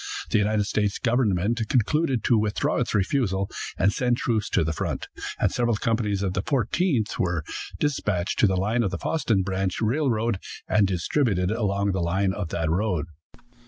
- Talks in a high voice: No, low, 105 Hz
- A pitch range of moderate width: Yes, average, 3.8 semitones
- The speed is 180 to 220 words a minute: No, average, 170 wpm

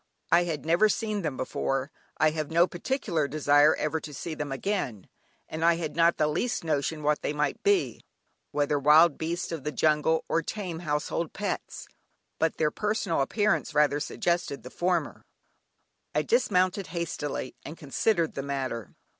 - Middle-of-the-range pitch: Yes, medium, 160 Hz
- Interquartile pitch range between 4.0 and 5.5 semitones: No, average, 2.9 semitones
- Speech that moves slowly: No, average, 165 wpm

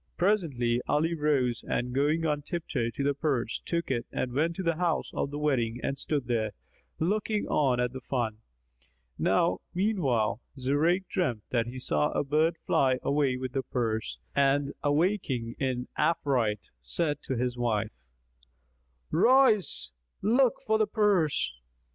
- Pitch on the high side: No, medium, 140 Hz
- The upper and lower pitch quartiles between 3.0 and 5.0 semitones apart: No, wide, 5.4 semitones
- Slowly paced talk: No, average, 150 wpm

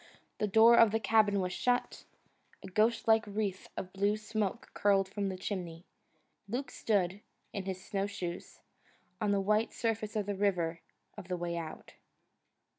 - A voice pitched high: Yes, high, 200 Hz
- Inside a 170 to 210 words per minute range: No, average, 155 wpm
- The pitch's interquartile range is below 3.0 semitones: Yes, narrow, 2.5 semitones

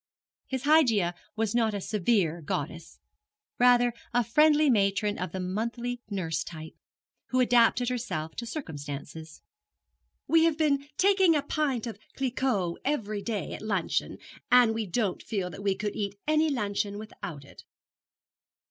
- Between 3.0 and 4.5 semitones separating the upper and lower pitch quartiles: No, average, 5.1 semitones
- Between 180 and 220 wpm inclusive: No, average, 145 wpm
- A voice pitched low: No, high, 220 Hz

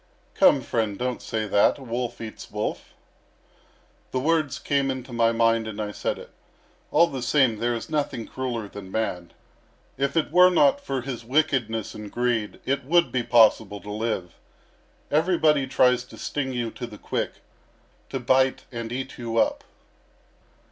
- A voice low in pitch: Yes, low, 120 Hz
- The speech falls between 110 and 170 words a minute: Yes, average, 165 wpm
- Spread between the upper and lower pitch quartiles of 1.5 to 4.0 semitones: Yes, average, 3.5 semitones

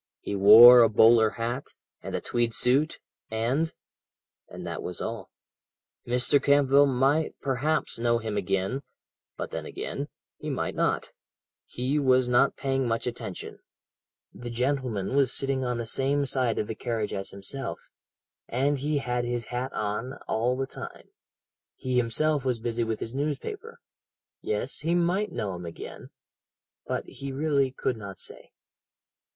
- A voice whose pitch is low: Yes, low, 125 Hz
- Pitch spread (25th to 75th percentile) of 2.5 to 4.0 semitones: Yes, average, 3.2 semitones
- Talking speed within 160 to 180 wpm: No, average, 150 wpm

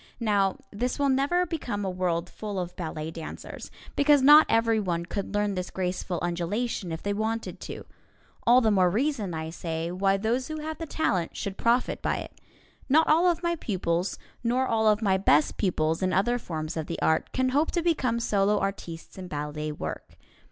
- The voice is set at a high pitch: Yes, high, 205 Hz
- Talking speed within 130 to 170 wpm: No, average, 190 wpm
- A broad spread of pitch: Yes, wide, 6.3 semitones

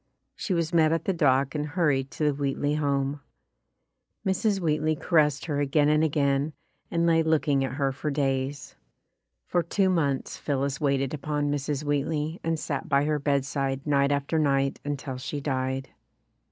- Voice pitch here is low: No, medium, 145 Hz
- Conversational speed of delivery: Yes, average, 165 wpm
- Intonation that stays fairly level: Yes, narrow, 2.1 semitones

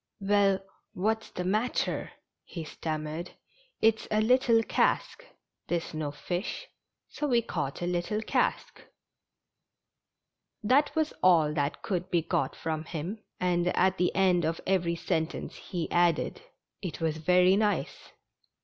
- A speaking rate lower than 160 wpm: Yes, average, 140 wpm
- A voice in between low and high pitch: Yes, medium, 180 Hz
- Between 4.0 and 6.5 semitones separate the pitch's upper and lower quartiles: Yes, average, 4.4 semitones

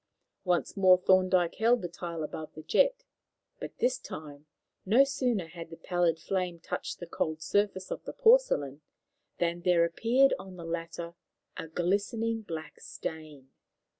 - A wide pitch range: No, average, 3.9 semitones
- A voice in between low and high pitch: Yes, medium, 175 Hz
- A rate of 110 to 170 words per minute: Yes, average, 150 wpm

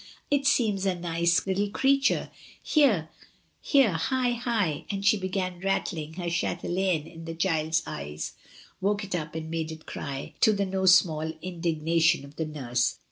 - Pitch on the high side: No, medium, 175 Hz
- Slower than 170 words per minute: Yes, average, 160 wpm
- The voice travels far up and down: No, average, 3.8 semitones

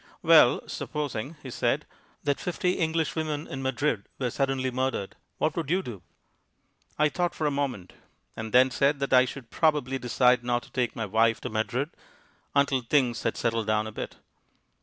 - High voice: No, low, 130 Hz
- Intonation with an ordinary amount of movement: Yes, average, 3.9 semitones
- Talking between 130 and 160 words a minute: No, average, 180 wpm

